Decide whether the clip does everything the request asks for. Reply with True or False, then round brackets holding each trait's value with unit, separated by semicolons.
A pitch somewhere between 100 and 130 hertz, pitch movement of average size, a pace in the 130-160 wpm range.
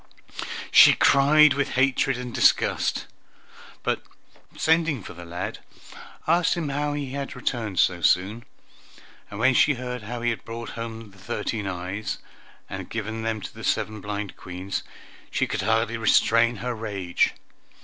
True (115 Hz; 4.4 semitones; 150 wpm)